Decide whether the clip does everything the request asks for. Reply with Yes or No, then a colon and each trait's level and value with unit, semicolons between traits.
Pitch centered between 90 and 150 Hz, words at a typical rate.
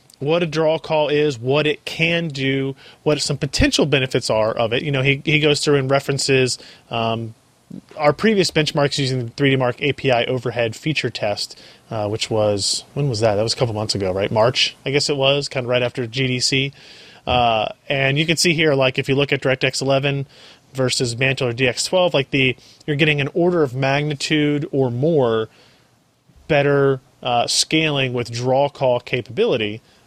Yes: low, 135 Hz; average, 185 wpm